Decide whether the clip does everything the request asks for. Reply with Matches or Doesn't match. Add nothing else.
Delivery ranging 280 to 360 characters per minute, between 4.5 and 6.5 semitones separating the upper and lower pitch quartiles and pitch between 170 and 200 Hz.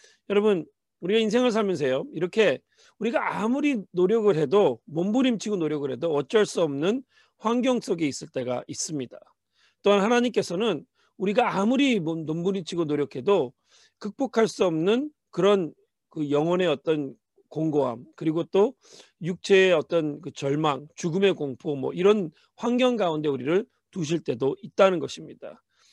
Matches